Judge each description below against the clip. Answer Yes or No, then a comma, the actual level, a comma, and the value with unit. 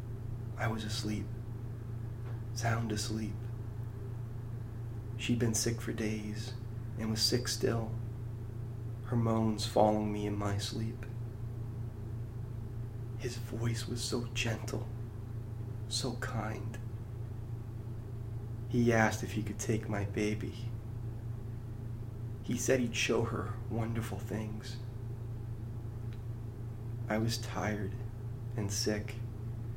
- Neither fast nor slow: No, slow, 95 wpm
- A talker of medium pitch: No, low, 115 Hz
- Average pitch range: No, narrow, 0.6 semitones